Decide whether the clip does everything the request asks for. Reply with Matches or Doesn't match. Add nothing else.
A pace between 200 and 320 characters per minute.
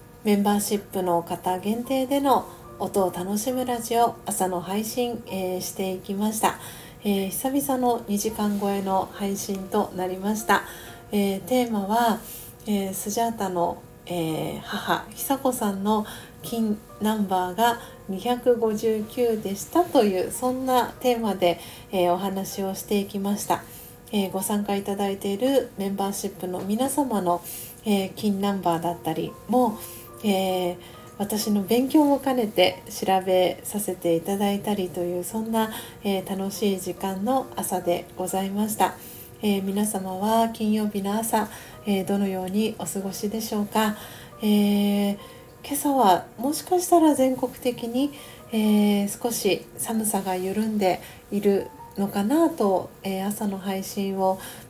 Matches